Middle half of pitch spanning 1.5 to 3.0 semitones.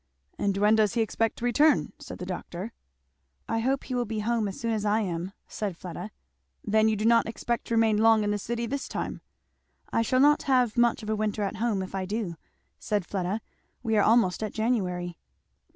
Yes: narrow, 2.4 semitones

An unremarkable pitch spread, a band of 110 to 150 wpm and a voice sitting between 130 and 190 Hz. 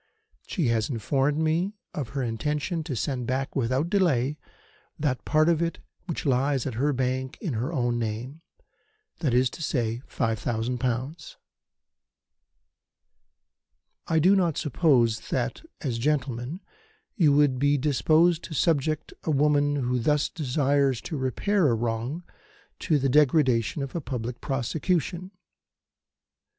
Yes: average, 4.0 semitones; average, 140 wpm; medium, 140 Hz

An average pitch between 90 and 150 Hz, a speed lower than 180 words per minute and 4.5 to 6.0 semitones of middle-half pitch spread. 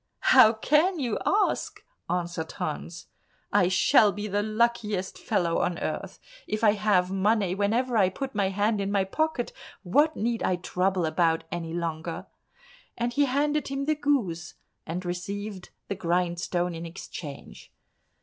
No: high, 200 Hz; average, 150 wpm; average, 5.1 semitones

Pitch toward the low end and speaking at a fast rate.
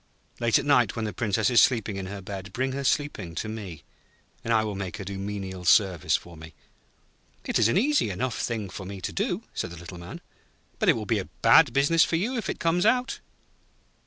Yes: low, 105 Hz; fast, 225 wpm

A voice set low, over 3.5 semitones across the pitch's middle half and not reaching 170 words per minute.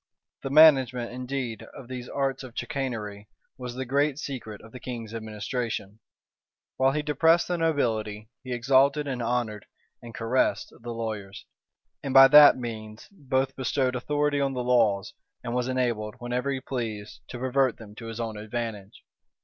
No: low, 125 Hz; average, 3.2 semitones; average, 160 wpm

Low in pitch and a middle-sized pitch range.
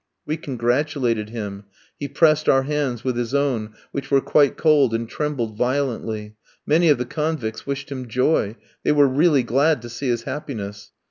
Yes: low, 130 Hz; average, 4.1 semitones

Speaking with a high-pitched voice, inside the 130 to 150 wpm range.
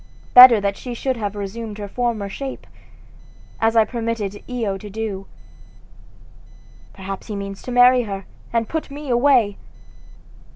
Yes: high, 225 Hz; average, 140 wpm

